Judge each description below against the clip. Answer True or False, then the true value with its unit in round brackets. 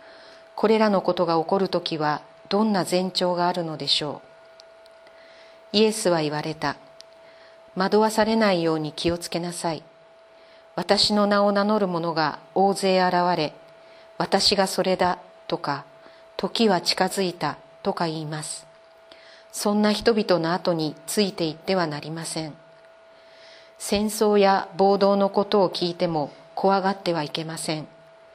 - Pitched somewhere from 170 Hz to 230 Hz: True (185 Hz)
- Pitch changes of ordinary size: True (4.3 semitones)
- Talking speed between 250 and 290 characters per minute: True (265 characters per minute)